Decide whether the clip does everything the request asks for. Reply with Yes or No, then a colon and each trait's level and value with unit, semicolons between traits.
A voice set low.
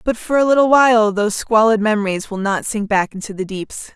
No: high, 215 Hz